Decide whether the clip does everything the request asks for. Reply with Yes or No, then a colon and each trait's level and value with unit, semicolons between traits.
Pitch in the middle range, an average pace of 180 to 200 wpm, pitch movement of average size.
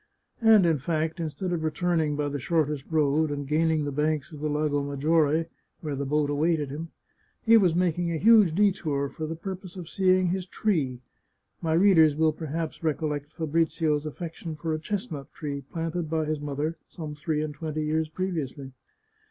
No: medium, 155 Hz; average, 185 wpm; narrow, 2.2 semitones